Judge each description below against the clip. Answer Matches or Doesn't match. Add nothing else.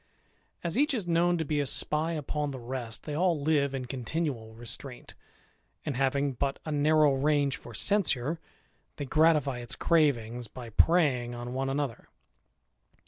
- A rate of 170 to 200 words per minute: Doesn't match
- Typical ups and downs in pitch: Matches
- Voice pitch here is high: Doesn't match